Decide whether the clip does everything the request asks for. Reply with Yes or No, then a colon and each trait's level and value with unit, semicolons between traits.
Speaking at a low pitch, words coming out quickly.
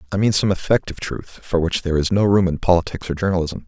Yes: very low, 90 Hz; fast, 245 wpm